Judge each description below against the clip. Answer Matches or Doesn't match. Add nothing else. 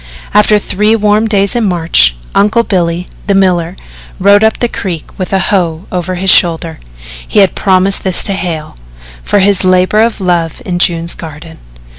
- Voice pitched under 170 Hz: Doesn't match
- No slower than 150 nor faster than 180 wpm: Matches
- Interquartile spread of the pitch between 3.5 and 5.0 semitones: Doesn't match